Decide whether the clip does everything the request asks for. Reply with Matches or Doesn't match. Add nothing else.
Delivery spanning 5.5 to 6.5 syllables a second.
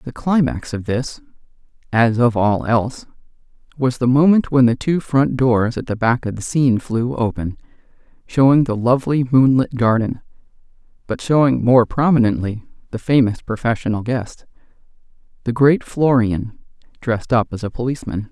Doesn't match